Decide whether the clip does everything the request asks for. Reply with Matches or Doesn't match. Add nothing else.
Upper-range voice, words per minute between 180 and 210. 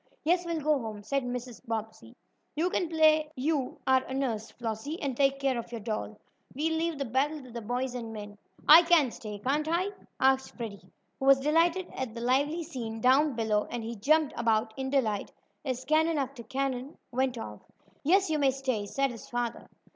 Matches